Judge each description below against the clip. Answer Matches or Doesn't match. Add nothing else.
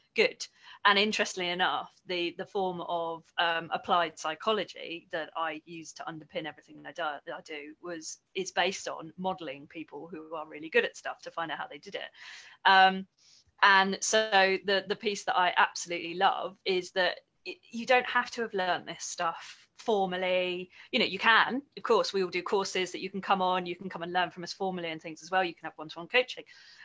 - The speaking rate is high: Matches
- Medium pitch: Matches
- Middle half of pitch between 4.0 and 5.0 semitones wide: Doesn't match